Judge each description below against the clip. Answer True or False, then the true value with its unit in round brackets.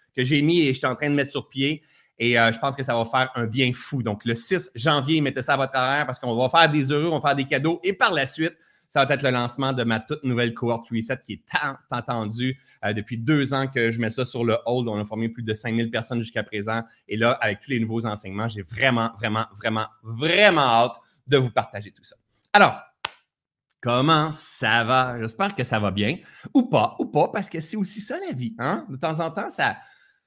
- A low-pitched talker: True (130 Hz)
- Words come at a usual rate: False (250 wpm)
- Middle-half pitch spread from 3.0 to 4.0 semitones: False (4.5 semitones)